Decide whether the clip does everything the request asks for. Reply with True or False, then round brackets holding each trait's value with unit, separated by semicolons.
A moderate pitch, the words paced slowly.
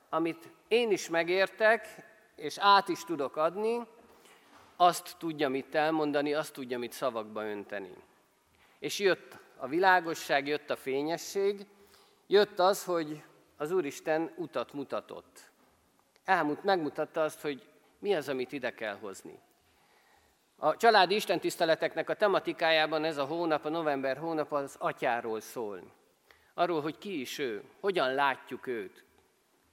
False (165 Hz; 130 wpm)